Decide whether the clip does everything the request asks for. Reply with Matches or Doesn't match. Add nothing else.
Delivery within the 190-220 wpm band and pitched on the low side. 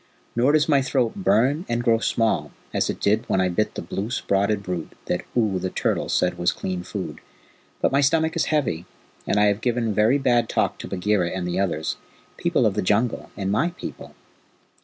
Matches